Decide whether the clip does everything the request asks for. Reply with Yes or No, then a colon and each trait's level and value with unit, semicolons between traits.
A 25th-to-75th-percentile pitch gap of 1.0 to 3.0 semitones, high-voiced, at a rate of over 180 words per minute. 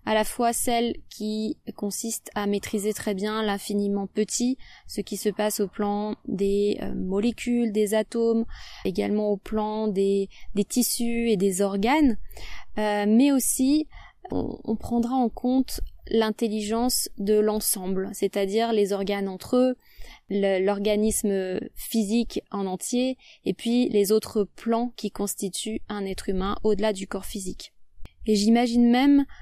No: narrow, 2.5 semitones; high, 215 Hz; slow, 145 wpm